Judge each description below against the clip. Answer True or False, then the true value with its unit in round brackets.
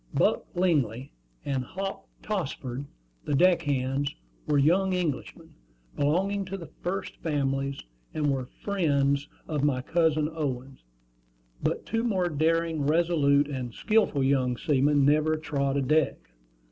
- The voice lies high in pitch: False (150 Hz)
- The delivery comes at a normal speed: False (130 wpm)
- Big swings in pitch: False (3.8 semitones)